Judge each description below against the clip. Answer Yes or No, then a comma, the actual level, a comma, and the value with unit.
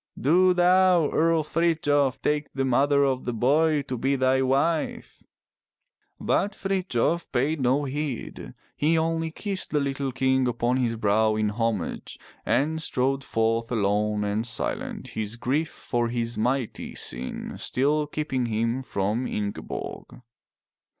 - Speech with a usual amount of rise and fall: Yes, average, 4.8 semitones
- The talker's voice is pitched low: Yes, low, 130 Hz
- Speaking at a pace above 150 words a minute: No, slow, 135 wpm